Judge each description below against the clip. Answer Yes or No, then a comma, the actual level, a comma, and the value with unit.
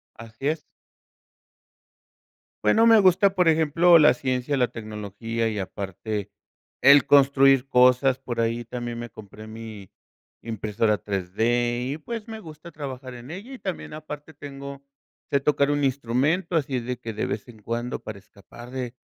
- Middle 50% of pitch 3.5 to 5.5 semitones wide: Yes, average, 4.3 semitones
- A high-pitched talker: No, low, 125 Hz